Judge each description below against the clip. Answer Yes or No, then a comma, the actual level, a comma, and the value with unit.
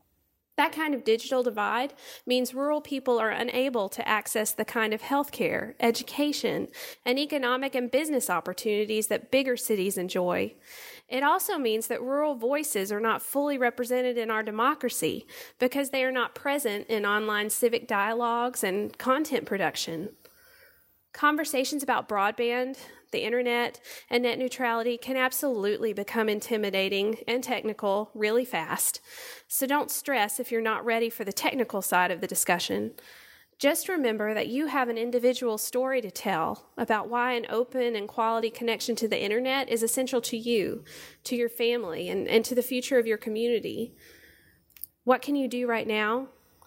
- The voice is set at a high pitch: Yes, high, 240 Hz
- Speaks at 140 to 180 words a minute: Yes, average, 155 wpm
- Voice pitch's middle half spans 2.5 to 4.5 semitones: Yes, average, 3.0 semitones